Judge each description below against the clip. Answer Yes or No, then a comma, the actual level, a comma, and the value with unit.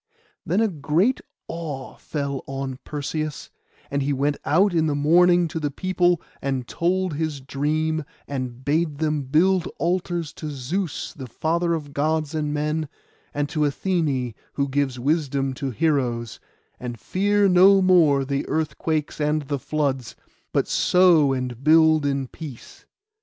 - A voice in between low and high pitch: Yes, medium, 150 Hz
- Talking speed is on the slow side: No, average, 145 wpm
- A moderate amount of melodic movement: Yes, average, 3.3 semitones